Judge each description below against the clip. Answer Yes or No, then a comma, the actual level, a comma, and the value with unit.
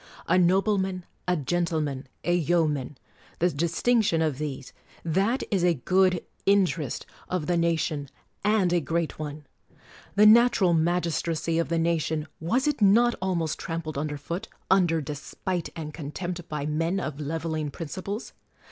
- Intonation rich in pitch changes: No, average, 3.3 semitones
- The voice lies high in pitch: No, medium, 170 Hz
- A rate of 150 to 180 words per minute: No, average, 140 wpm